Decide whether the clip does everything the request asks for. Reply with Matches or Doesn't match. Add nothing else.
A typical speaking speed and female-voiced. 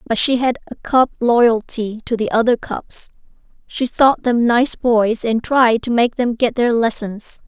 Matches